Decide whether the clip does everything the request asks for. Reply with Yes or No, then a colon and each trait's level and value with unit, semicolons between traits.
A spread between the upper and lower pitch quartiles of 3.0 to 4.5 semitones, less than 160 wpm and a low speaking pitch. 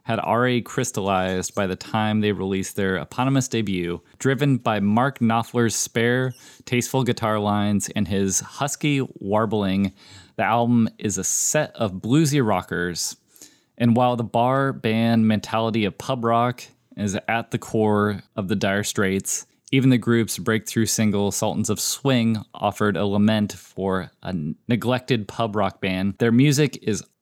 Yes: average, 3.3 semitones; average, 150 wpm; low, 110 Hz